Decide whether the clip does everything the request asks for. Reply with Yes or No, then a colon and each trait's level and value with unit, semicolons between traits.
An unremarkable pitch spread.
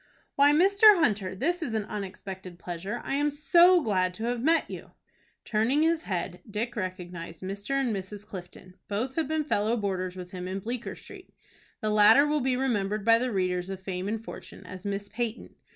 No: wide, 6.1 semitones